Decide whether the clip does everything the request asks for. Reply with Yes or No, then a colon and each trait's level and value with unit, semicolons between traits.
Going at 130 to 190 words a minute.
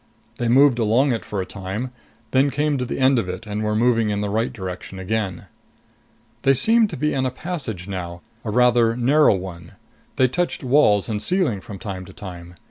No: fast, 205 wpm